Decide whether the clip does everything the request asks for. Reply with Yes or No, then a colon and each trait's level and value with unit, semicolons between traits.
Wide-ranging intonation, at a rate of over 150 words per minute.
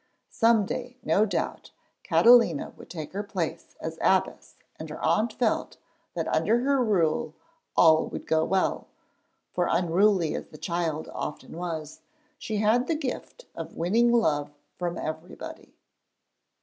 No: wide, 6.3 semitones; average, 140 wpm